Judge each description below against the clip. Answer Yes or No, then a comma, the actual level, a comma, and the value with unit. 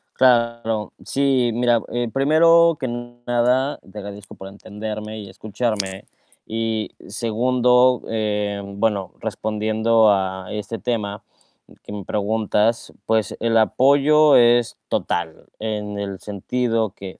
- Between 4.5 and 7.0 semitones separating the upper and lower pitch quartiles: No, average, 2.8 semitones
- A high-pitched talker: No, low, 110 Hz